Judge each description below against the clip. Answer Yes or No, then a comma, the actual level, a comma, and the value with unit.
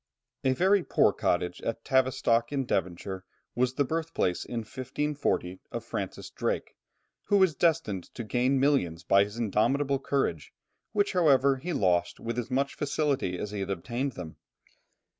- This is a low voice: Yes, low, 125 Hz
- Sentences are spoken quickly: No, average, 155 wpm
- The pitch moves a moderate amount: No, wide, 6.3 semitones